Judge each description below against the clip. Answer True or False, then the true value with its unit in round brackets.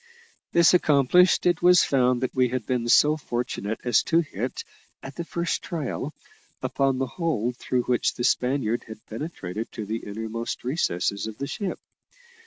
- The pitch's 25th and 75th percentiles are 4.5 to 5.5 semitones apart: True (5.0 semitones)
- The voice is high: False (125 Hz)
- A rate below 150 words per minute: False (165 wpm)